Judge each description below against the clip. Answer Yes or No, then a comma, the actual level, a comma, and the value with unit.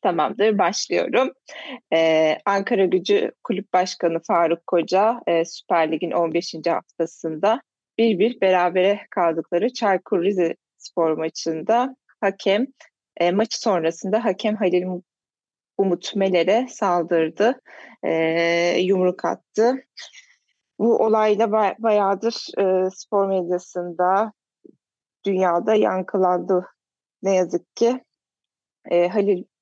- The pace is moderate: No, slow, 90 wpm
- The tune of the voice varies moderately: Yes, average, 4.1 semitones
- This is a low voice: No, high, 190 Hz